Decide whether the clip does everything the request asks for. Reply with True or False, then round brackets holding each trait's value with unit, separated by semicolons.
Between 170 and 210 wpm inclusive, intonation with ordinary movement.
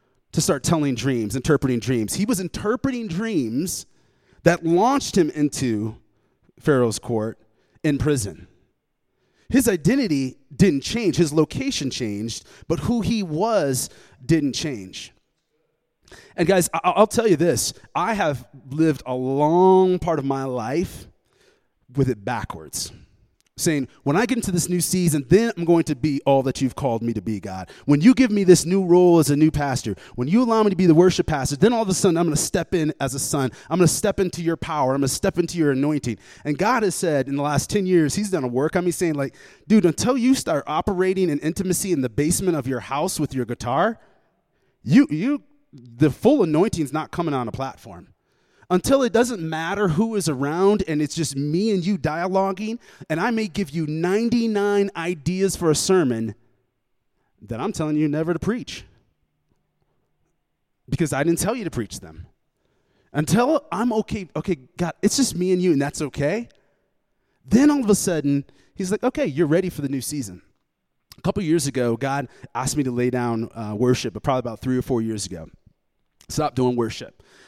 False (195 wpm; 6.1 semitones)